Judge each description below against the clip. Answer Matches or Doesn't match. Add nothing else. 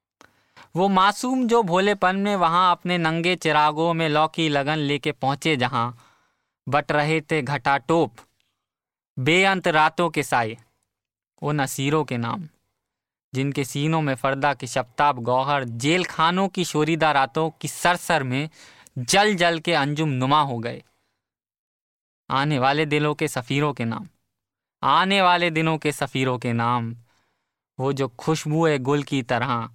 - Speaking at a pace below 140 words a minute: Doesn't match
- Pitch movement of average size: Matches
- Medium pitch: Matches